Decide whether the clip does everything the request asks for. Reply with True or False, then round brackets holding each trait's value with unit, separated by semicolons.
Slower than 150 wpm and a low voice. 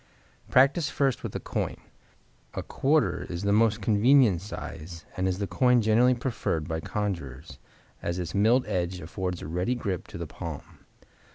False (165 wpm; 100 Hz)